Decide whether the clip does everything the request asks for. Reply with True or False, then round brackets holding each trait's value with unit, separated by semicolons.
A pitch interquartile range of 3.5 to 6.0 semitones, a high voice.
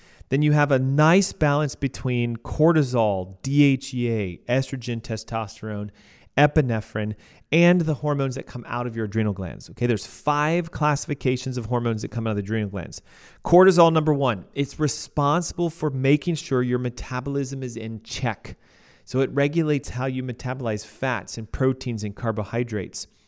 False (4.6 semitones; 125 Hz)